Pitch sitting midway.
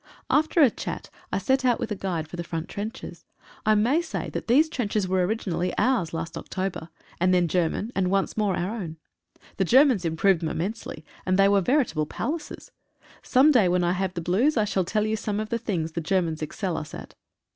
No: high, 195 Hz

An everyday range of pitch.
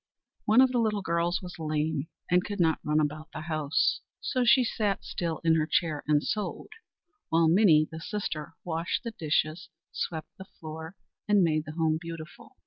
Yes: average, 4.0 semitones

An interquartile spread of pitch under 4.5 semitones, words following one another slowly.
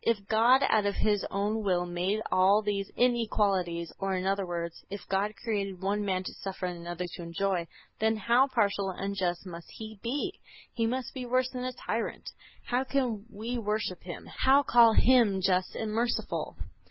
No: average, 3.8 semitones; average, 185 wpm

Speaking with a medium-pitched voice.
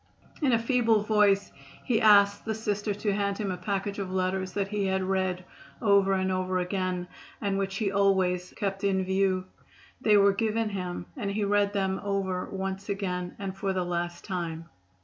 No: high, 195 Hz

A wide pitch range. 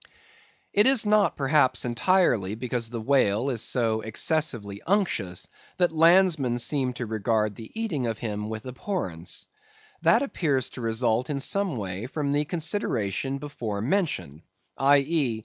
Yes: wide, 6.1 semitones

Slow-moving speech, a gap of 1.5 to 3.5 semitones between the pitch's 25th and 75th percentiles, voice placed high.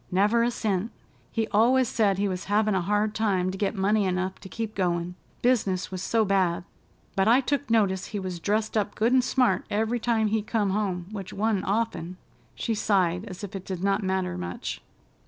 No: average, 200 wpm; average, 2.8 semitones; high, 205 Hz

